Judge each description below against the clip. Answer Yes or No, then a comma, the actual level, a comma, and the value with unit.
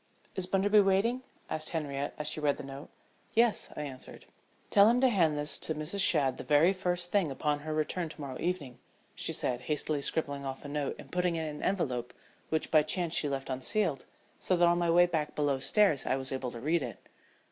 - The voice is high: No, medium, 155 Hz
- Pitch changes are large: No, average, 4.2 semitones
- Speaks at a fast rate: Yes, fast, 220 wpm